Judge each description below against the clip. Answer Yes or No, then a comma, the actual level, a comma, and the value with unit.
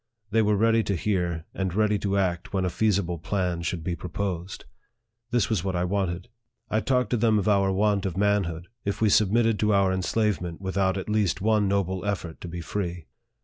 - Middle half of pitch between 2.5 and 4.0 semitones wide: Yes, average, 2.9 semitones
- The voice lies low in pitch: Yes, low, 100 Hz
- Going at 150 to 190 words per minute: No, average, 200 wpm